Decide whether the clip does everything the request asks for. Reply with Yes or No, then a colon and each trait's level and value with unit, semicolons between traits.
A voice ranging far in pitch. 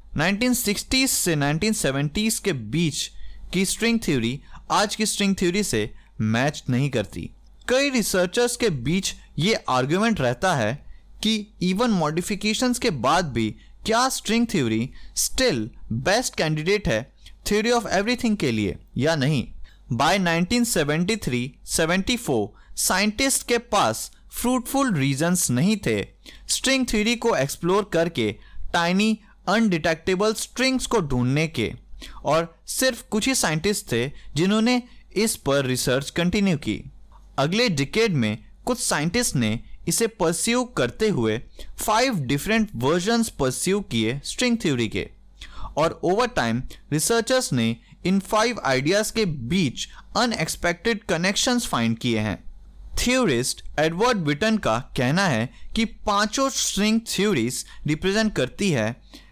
Yes: wide, 8.4 semitones